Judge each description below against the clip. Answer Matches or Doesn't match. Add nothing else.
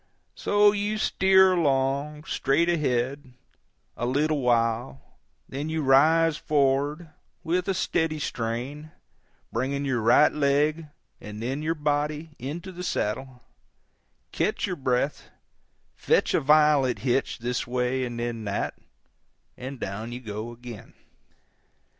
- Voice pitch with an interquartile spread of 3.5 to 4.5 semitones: Matches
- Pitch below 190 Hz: Matches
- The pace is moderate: Doesn't match